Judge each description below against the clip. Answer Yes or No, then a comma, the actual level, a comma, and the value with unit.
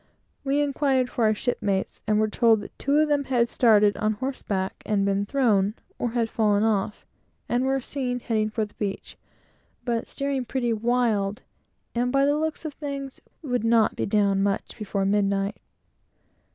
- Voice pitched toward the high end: Yes, high, 230 Hz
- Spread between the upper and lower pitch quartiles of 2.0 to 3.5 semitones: No, average, 4.1 semitones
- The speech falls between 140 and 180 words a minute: Yes, average, 175 wpm